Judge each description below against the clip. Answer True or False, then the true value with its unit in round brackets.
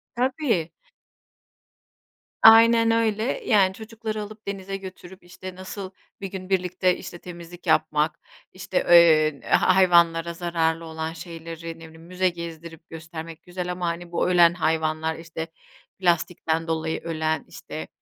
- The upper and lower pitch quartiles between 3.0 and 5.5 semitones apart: False (2.5 semitones)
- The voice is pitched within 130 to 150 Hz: False (175 Hz)